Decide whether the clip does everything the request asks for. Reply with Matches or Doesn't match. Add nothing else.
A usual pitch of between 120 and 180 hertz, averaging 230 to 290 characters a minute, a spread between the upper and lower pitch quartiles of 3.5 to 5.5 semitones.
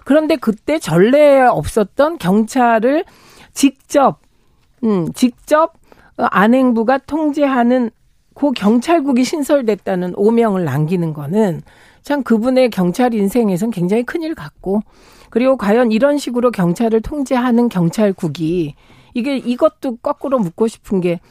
Doesn't match